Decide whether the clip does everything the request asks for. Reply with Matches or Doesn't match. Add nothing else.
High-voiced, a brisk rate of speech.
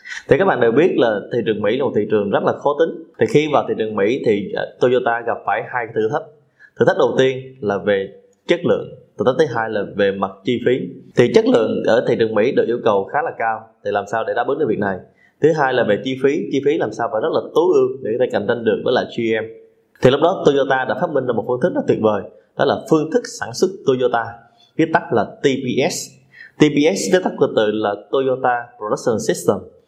Doesn't match